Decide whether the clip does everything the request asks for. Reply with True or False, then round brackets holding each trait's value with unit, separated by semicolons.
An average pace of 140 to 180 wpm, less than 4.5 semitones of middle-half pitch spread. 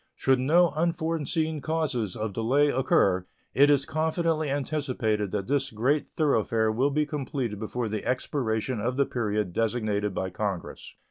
False (145 wpm; 5.5 semitones)